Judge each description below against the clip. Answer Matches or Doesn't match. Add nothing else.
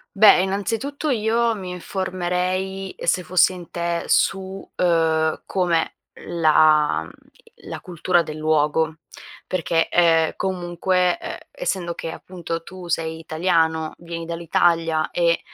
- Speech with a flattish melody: Matches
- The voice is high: Doesn't match